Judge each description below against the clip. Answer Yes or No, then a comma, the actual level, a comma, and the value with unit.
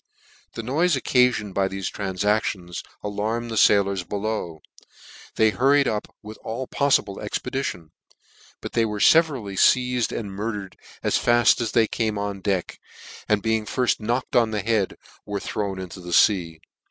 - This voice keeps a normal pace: Yes, average, 155 wpm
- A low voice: Yes, low, 105 Hz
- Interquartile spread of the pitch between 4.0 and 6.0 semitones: No, average, 3.2 semitones